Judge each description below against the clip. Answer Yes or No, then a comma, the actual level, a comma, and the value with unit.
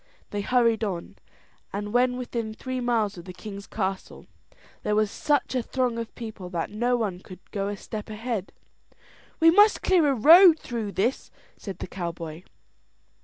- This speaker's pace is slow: No, average, 170 wpm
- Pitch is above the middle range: Yes, high, 220 Hz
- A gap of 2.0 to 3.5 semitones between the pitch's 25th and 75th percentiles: No, average, 4.0 semitones